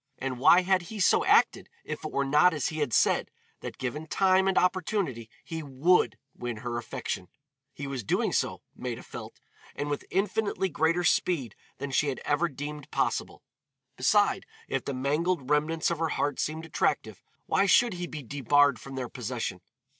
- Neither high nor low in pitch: Yes, medium, 150 Hz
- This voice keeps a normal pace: Yes, average, 175 wpm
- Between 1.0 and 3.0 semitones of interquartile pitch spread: No, average, 5.1 semitones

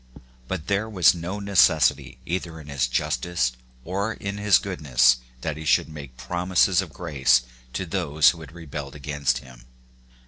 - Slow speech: No, average, 160 wpm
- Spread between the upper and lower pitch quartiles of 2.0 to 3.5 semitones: No, average, 5.2 semitones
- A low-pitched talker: Yes, very low, 80 Hz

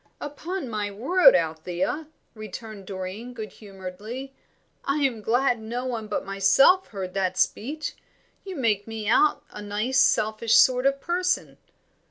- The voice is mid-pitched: No, high, 225 Hz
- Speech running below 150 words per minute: Yes, average, 140 wpm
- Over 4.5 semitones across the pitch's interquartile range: Yes, average, 5.2 semitones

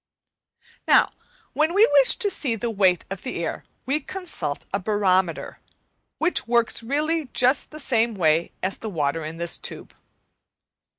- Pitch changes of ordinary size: No, wide, 8.2 semitones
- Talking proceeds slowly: No, average, 160 wpm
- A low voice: No, high, 225 Hz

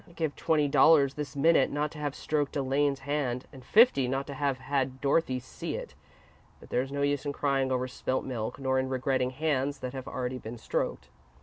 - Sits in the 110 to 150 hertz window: Yes, low, 135 Hz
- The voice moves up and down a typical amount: No, narrow, 2.0 semitones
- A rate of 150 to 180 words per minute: No, fast, 205 wpm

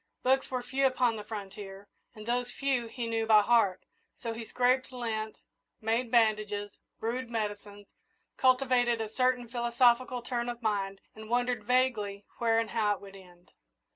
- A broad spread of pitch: No, average, 2.8 semitones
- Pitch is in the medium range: No, high, 230 Hz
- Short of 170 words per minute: Yes, average, 160 wpm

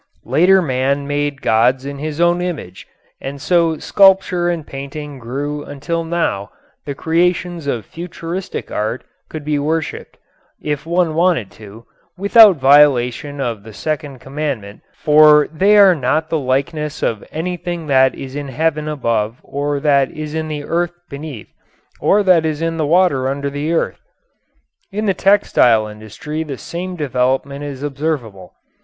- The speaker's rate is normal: Yes, average, 150 wpm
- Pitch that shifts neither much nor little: Yes, average, 3.8 semitones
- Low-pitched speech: No, medium, 150 Hz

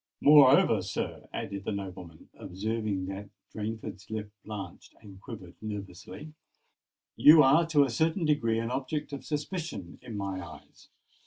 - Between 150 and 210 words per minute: No, average, 140 wpm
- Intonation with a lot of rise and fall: Yes, wide, 6.7 semitones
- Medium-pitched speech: No, low, 110 Hz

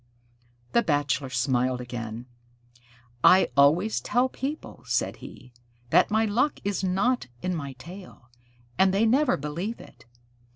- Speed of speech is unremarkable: No, slow, 130 wpm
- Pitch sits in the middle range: Yes, medium, 180 Hz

